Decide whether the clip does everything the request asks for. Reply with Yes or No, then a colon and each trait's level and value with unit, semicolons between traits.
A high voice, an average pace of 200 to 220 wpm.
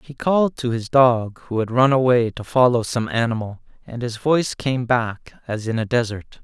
No: low, 120 Hz; fast, 205 wpm